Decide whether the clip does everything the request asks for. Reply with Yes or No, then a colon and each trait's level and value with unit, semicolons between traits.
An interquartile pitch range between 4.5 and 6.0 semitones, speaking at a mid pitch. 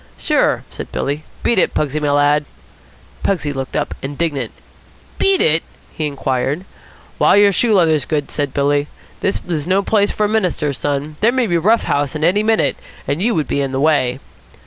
Yes: wide, 5.4 semitones; medium, 150 Hz